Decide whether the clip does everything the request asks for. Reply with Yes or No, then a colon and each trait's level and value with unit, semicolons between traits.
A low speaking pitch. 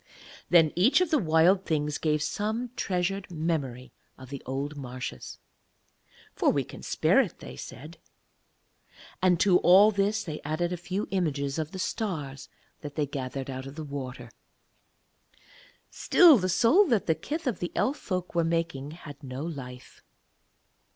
No: medium, 160 Hz